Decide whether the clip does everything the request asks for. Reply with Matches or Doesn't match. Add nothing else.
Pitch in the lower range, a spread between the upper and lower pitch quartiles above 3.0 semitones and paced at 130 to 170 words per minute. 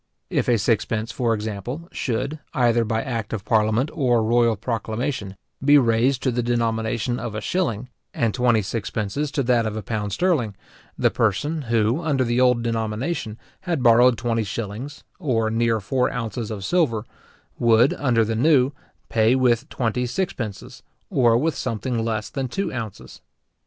Doesn't match